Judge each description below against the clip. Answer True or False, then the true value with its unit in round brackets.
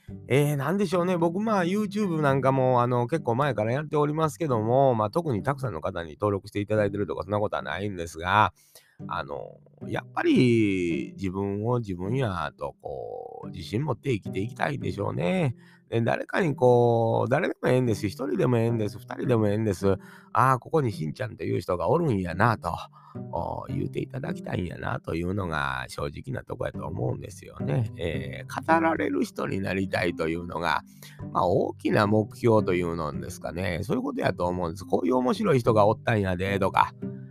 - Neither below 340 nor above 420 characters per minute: True (410 characters per minute)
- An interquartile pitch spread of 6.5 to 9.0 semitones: False (5.8 semitones)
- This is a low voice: True (115 Hz)